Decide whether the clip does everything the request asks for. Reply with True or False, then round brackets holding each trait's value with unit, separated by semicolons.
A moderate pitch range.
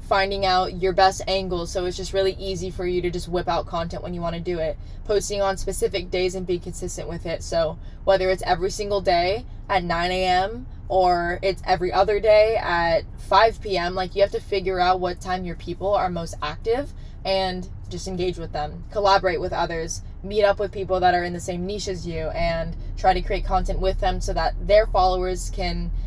False (1.6 semitones)